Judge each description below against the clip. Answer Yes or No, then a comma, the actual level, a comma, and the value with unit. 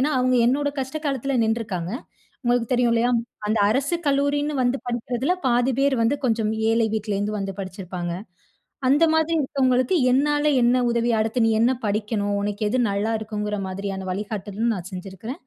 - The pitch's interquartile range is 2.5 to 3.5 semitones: No, average, 3.9 semitones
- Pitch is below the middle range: No, high, 230 Hz